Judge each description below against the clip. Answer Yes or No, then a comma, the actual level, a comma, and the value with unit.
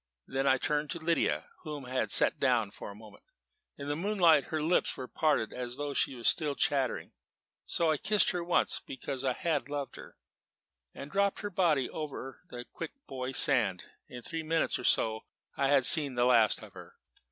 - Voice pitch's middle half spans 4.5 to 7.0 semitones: No, average, 4.0 semitones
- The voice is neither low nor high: Yes, medium, 145 Hz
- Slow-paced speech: No, average, 200 wpm